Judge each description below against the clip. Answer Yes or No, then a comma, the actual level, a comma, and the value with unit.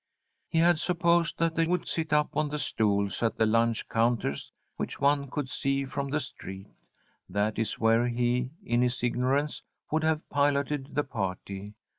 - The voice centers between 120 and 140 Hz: Yes, low, 135 Hz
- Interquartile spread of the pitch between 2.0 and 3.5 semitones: No, average, 4.8 semitones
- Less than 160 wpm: No, average, 170 wpm